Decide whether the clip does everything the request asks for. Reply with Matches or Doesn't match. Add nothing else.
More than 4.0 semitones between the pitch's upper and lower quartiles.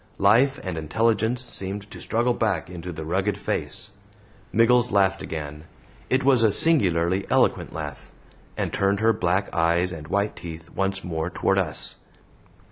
Matches